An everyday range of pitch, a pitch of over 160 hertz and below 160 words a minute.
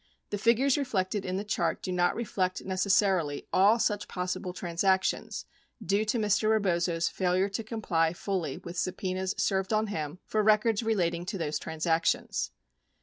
Yes: average, 3.2 semitones; high, 190 Hz; average, 150 wpm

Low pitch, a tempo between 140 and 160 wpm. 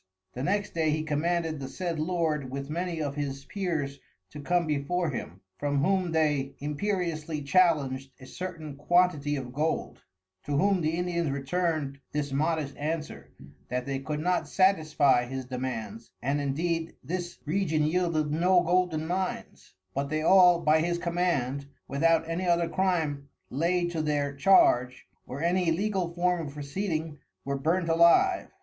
No: medium, 155 Hz; average, 155 wpm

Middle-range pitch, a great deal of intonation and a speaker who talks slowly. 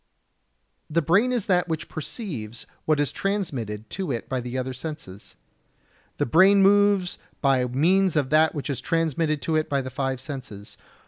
No: medium, 150 Hz; wide, 5.7 semitones; average, 170 wpm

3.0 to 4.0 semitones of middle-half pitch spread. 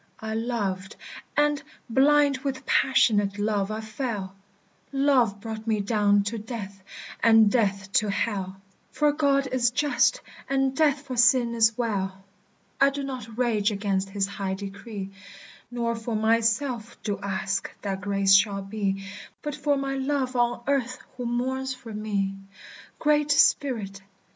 No: average, 4.7 semitones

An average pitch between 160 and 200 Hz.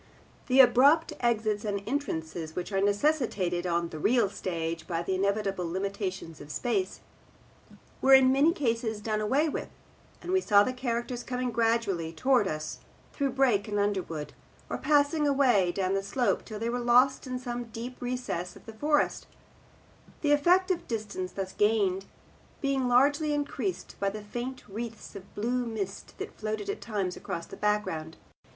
No: high, 220 Hz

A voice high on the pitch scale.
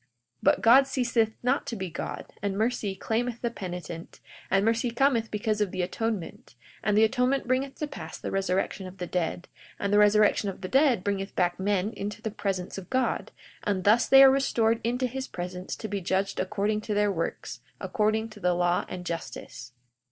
Yes: high, 210 Hz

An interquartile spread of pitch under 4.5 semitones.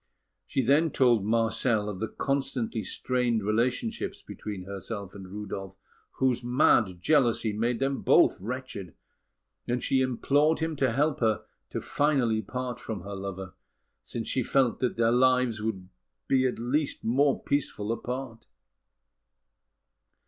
Yes: average, 3.7 semitones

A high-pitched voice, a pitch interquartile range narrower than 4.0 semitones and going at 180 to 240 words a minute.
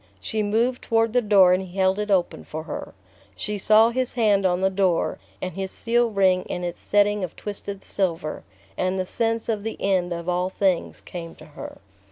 Yes: high, 195 Hz; average, 2.8 semitones; fast, 205 wpm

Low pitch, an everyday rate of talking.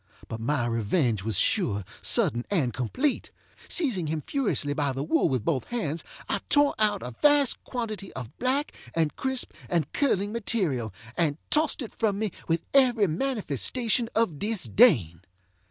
No: medium, 185 Hz; average, 155 wpm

